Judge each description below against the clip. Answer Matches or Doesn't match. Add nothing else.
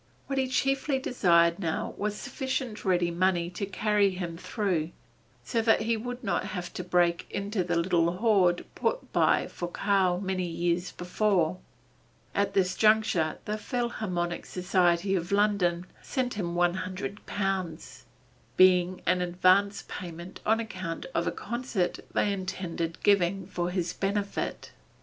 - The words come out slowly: Doesn't match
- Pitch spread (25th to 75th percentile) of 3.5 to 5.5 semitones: Doesn't match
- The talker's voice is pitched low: Doesn't match